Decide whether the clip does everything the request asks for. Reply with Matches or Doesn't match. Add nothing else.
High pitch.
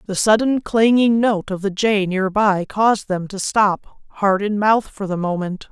Matches